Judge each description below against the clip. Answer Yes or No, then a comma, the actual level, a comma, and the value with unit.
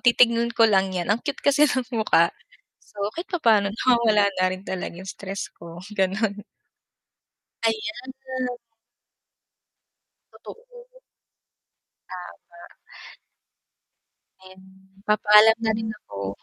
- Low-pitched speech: No, high, 210 Hz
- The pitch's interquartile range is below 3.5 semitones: No, average, 3.8 semitones